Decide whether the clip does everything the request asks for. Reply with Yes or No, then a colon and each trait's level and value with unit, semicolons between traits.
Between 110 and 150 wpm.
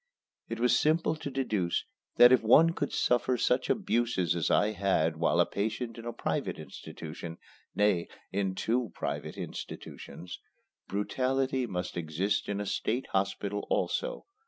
Yes: average, 145 wpm